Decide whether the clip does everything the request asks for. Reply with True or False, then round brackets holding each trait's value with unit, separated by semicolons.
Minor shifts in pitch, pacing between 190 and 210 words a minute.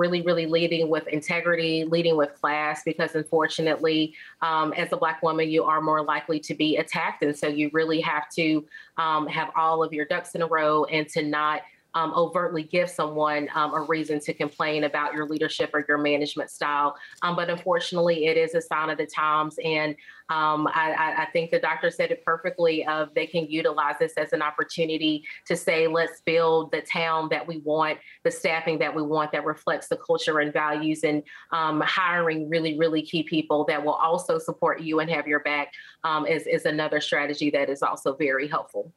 True (1.5 semitones; 200 wpm)